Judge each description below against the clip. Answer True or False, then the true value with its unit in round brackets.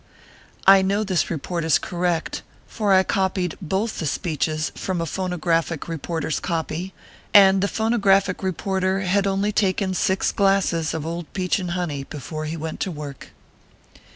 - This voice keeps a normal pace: True (155 wpm)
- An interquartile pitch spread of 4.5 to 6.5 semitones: False (3.0 semitones)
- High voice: False (180 Hz)